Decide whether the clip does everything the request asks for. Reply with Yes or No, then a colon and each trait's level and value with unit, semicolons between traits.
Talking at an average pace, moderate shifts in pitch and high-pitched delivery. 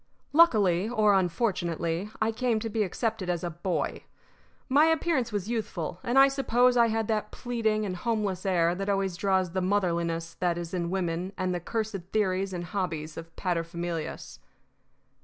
Yes: average, 165 wpm; average, 4.3 semitones; high, 195 Hz